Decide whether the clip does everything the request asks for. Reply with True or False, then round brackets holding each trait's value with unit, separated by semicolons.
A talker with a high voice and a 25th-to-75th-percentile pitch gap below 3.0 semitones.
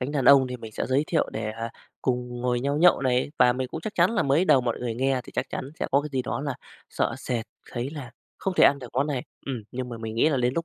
False (130 Hz; 2.5 semitones)